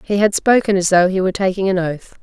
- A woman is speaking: Yes, female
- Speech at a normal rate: No, fast, 270 wpm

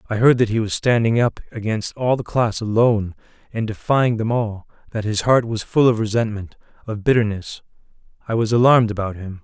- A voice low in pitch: Yes, low, 110 Hz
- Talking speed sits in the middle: Yes, average, 185 wpm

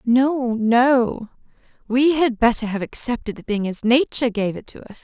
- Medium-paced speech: Yes, average, 180 wpm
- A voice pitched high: Yes, high, 240 Hz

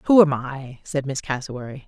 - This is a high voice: No, medium, 140 Hz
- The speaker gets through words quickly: No, average, 190 wpm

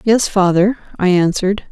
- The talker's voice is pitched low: No, high, 195 Hz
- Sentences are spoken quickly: No, average, 140 wpm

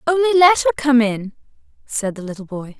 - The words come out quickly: No, average, 195 wpm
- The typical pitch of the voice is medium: No, very high, 260 Hz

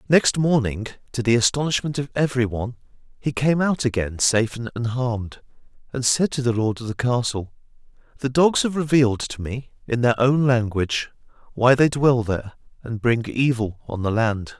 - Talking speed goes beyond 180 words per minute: No, average, 175 wpm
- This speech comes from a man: Yes, male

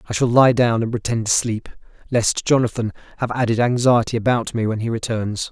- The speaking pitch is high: No, low, 115 Hz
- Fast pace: No, average, 195 wpm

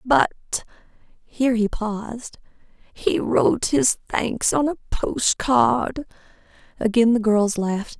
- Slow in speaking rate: Yes, slow, 115 wpm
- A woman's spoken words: Yes, female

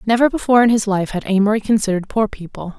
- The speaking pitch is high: Yes, high, 210 Hz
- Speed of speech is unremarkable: No, fast, 215 wpm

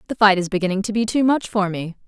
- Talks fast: Yes, fast, 290 wpm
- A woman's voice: Yes, female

